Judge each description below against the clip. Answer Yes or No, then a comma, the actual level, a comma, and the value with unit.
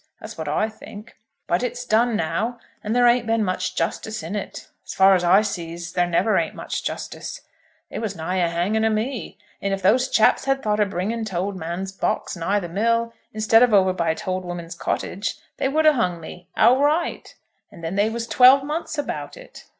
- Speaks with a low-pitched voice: No, high, 210 Hz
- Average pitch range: Yes, average, 4.6 semitones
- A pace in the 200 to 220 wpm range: Yes, fast, 205 wpm